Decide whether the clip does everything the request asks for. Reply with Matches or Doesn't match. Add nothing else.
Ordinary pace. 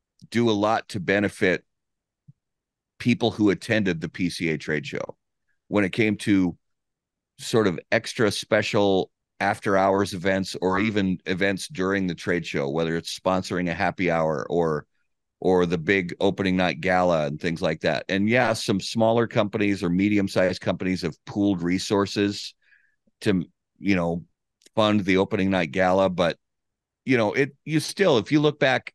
Matches